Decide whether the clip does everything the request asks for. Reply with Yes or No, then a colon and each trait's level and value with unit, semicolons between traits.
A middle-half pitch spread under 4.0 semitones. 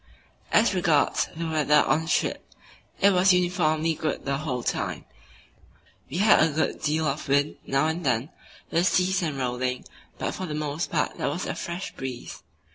Yes: average, 3.6 semitones